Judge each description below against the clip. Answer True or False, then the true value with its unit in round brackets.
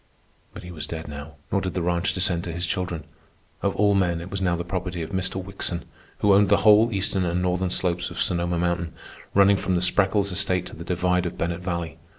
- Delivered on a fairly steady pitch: True (2.0 semitones)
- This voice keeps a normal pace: False (225 wpm)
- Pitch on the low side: True (90 Hz)